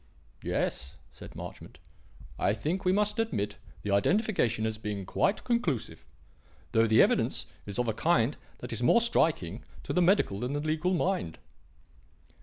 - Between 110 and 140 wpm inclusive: No, average, 160 wpm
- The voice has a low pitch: Yes, low, 125 Hz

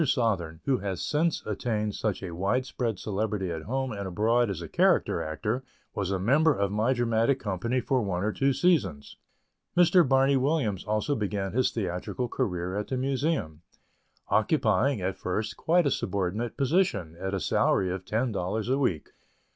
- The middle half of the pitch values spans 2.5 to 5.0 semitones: No, wide, 5.5 semitones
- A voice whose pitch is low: Yes, low, 110 Hz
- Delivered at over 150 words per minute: Yes, average, 170 wpm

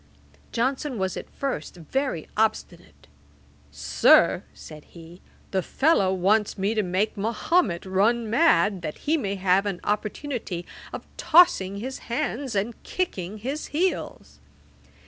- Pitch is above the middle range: Yes, high, 205 Hz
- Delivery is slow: Yes, slow, 125 wpm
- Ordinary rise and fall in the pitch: No, wide, 6.2 semitones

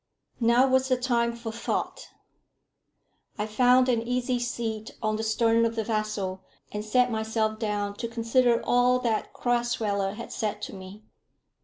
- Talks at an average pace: Yes, average, 155 wpm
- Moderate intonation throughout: No, narrow, 2.1 semitones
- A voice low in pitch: No, high, 230 Hz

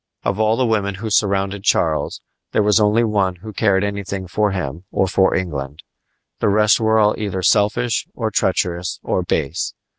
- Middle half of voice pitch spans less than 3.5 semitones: Yes, narrow, 2.5 semitones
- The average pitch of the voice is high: No, low, 100 Hz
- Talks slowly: No, average, 175 wpm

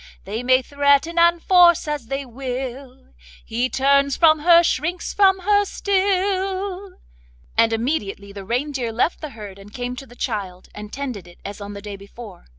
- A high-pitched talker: Yes, very high, 270 Hz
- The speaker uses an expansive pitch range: Yes, wide, 7.3 semitones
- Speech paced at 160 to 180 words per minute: Yes, average, 170 wpm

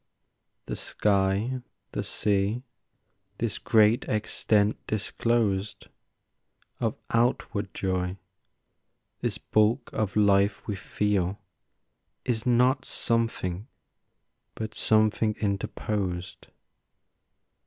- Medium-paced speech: No, slow, 80 wpm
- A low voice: Yes, low, 105 Hz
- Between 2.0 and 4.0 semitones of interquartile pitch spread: Yes, narrow, 2.5 semitones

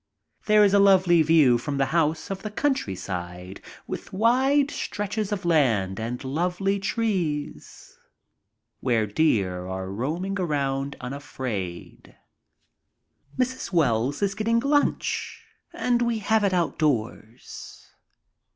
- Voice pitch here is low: No, medium, 160 Hz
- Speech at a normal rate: No, slow, 115 wpm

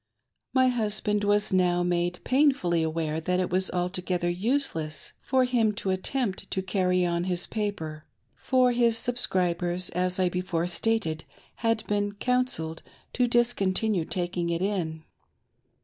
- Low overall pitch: No, medium, 185 Hz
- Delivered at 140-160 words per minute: Yes, average, 145 wpm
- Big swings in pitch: No, average, 4.4 semitones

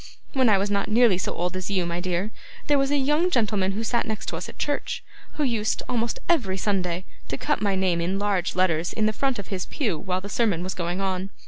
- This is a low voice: No, high, 200 Hz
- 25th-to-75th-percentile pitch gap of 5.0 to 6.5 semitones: No, average, 4.1 semitones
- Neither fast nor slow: No, fast, 240 wpm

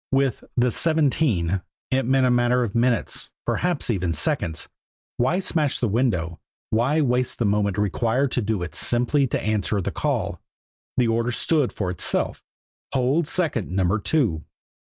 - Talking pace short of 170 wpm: Yes, average, 155 wpm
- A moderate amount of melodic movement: Yes, average, 4.7 semitones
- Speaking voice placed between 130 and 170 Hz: No, low, 120 Hz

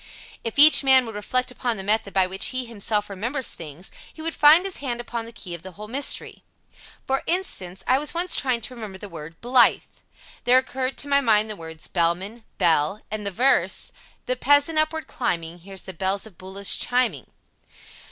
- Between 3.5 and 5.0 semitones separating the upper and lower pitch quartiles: No, wide, 5.5 semitones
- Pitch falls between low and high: No, high, 225 Hz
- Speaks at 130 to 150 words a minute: No, average, 200 wpm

